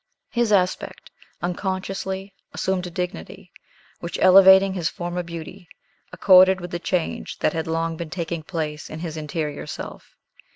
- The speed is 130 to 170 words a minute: Yes, average, 140 wpm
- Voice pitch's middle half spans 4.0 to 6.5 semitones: No, narrow, 2.6 semitones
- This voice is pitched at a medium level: Yes, medium, 175 Hz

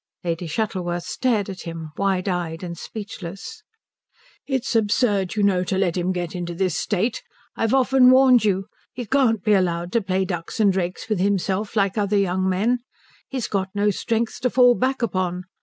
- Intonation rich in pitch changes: No, average, 3.9 semitones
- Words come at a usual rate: Yes, average, 180 wpm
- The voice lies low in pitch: No, high, 195 Hz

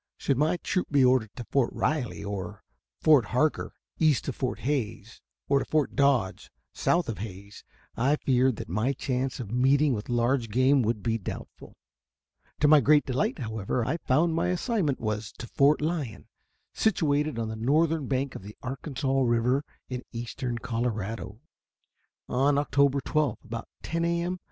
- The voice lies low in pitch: Yes, low, 130 Hz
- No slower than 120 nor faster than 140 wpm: No, average, 165 wpm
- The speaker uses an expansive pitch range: No, average, 4.2 semitones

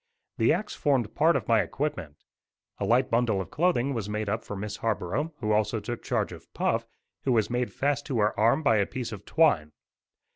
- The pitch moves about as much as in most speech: Yes, average, 4.6 semitones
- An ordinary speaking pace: No, fast, 210 wpm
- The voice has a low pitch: Yes, low, 115 Hz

